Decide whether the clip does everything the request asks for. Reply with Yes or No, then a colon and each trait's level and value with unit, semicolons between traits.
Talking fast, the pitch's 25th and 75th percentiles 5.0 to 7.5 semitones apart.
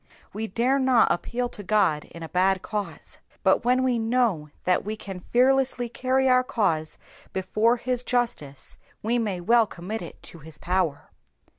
No: average, 165 wpm; wide, 5.4 semitones